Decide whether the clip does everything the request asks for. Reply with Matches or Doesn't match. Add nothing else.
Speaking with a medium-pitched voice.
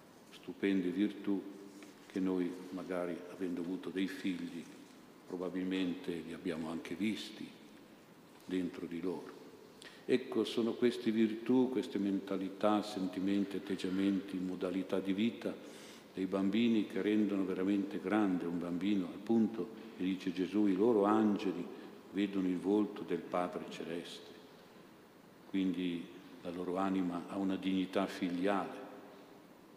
Doesn't match